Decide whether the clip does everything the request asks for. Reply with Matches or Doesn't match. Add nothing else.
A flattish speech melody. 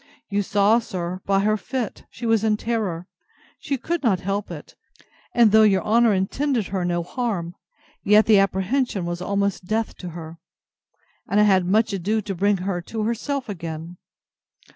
Doesn't match